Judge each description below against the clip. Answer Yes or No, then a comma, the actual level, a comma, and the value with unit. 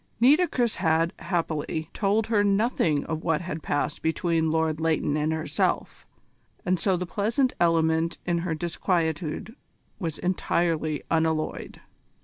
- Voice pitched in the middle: Yes, medium, 165 Hz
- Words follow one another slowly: Yes, slow, 125 wpm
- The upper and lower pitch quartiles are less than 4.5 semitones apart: Yes, average, 2.8 semitones